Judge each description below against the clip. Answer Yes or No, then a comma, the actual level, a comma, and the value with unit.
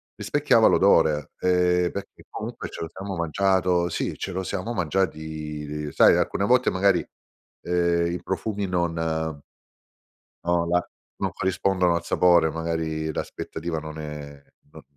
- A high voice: No, very low, 85 Hz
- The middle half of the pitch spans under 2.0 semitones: No, average, 2.8 semitones